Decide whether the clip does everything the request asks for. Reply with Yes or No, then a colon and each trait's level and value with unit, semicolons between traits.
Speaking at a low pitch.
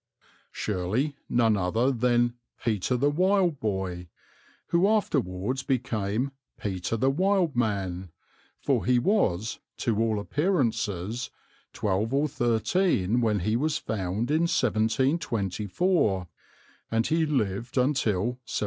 Yes: low, 120 Hz